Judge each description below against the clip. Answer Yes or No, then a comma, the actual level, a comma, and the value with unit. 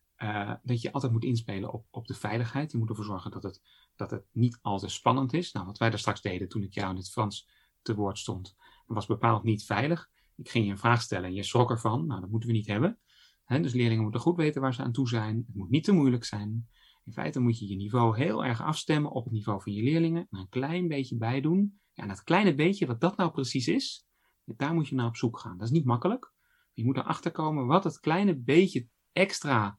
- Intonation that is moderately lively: No, wide, 5.9 semitones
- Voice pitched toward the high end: No, low, 120 Hz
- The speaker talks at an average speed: No, fast, 250 wpm